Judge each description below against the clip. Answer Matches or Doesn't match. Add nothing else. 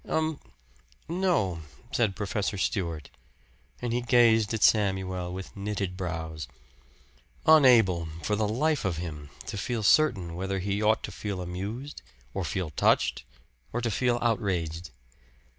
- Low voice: Matches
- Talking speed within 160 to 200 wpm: Doesn't match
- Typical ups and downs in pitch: Matches